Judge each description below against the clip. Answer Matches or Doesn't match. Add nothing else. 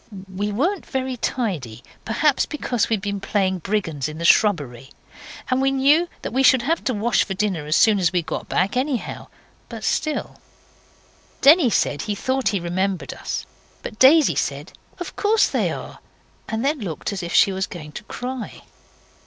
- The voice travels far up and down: Matches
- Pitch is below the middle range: Doesn't match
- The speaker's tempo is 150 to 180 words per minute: Matches